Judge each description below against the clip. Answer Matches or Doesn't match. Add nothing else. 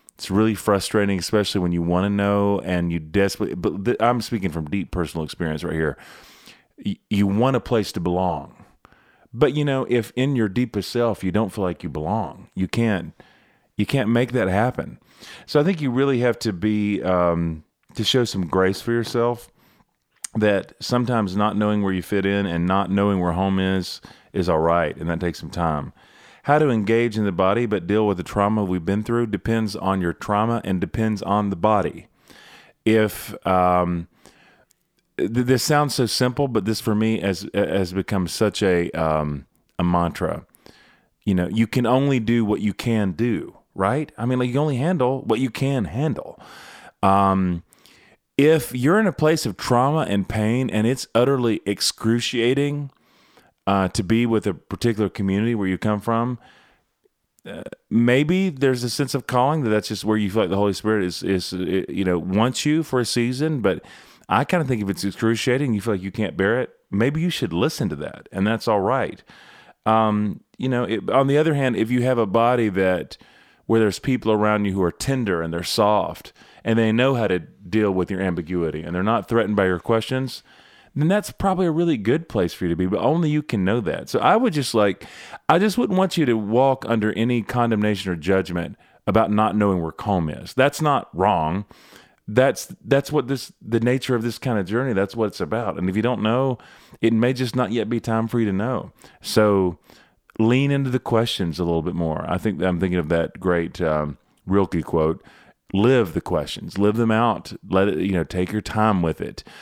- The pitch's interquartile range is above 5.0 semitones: Doesn't match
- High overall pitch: Doesn't match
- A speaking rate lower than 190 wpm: Doesn't match